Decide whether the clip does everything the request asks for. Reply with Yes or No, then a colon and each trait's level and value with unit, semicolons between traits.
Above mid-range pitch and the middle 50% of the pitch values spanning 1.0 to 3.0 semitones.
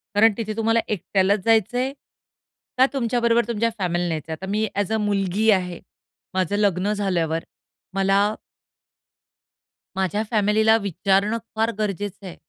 Yes: high, 205 Hz; average, 2.7 semitones